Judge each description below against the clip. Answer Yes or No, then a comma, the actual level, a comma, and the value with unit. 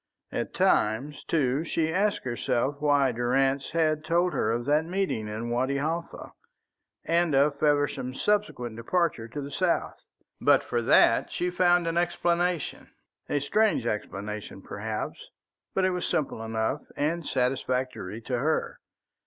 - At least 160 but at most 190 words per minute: No, average, 140 wpm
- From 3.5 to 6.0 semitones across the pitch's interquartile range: Yes, wide, 5.4 semitones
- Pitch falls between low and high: Yes, medium, 145 Hz